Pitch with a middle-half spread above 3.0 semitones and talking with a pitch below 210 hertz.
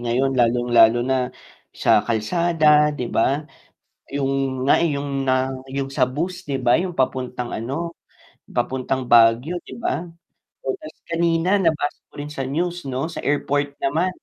Yes: average, 4.0 semitones; medium, 140 Hz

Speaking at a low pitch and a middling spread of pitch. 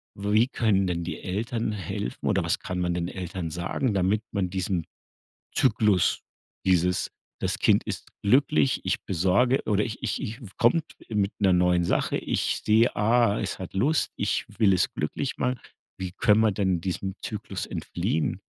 Yes: low, 100 Hz; average, 3.6 semitones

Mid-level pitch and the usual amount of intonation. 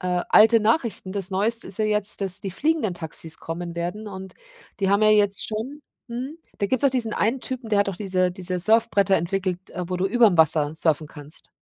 No: high, 195 Hz; average, 3.6 semitones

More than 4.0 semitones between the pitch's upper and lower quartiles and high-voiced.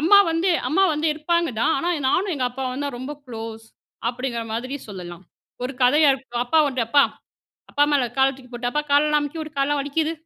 No: average, 3.4 semitones; very high, 275 Hz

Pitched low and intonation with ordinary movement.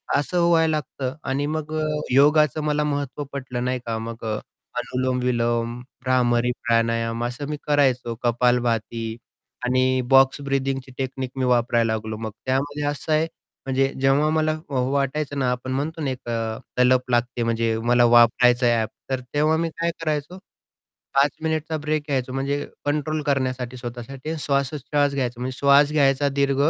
Yes: low, 130 Hz; average, 3.0 semitones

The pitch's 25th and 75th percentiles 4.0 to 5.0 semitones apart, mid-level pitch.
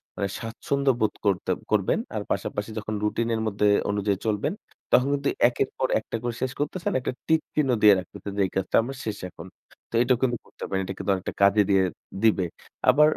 No: average, 4.6 semitones; low, 110 Hz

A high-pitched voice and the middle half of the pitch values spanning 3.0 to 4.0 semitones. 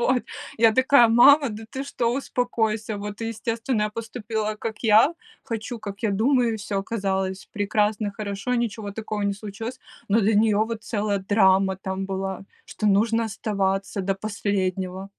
No: high, 215 Hz; narrow, 2.5 semitones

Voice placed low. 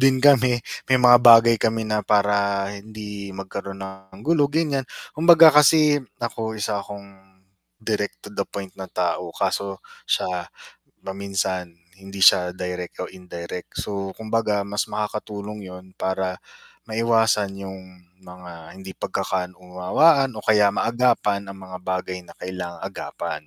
Yes: low, 100 Hz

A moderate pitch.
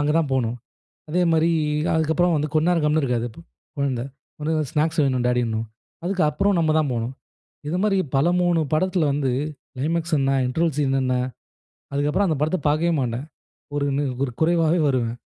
Yes: medium, 150 Hz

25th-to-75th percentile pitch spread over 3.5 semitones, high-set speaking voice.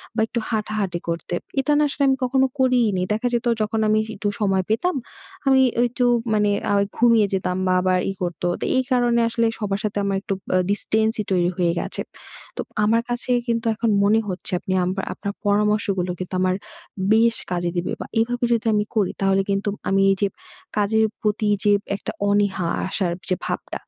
No: average, 3.2 semitones; high, 210 Hz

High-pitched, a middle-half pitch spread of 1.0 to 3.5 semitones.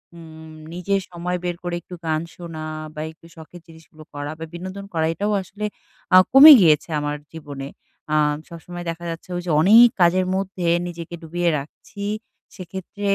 No: medium, 170 Hz; narrow, 2.5 semitones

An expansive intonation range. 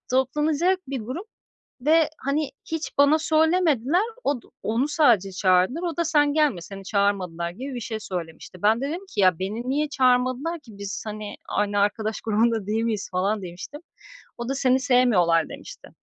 Yes: wide, 6.5 semitones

